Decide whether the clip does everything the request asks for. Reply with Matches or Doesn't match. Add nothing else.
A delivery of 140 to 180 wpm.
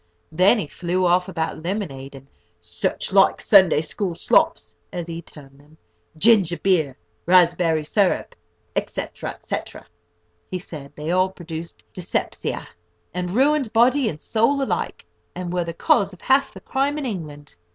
Matches